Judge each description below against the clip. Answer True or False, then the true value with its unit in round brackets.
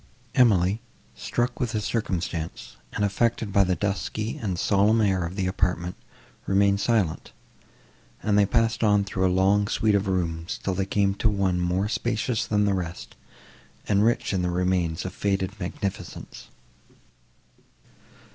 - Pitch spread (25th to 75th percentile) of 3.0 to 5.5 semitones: False (2.4 semitones)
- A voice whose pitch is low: True (100 Hz)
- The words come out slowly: False (150 wpm)